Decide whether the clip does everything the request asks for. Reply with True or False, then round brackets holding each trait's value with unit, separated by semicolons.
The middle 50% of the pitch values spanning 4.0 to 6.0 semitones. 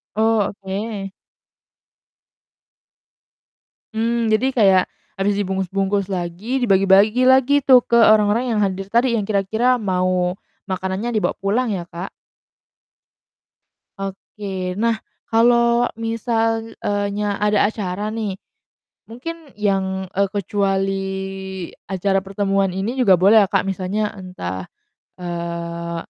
False (3.0 semitones)